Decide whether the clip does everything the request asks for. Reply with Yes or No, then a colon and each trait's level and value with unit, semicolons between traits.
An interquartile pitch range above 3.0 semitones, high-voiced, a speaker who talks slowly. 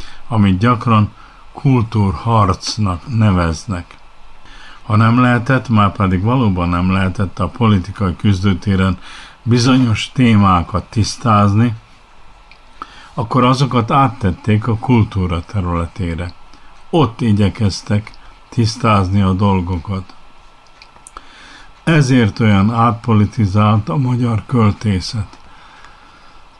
No: average, 3.7 semitones; low, 105 Hz; slow, 80 wpm